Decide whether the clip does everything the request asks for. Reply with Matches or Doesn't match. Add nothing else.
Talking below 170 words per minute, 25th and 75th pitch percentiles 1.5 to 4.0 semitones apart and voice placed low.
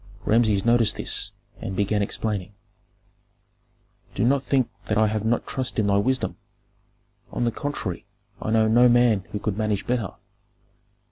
Matches